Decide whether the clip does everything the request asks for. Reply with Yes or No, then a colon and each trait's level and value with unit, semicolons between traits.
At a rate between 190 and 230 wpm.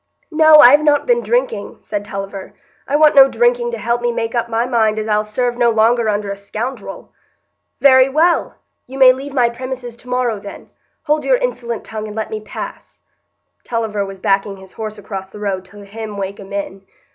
Yes: average, 195 wpm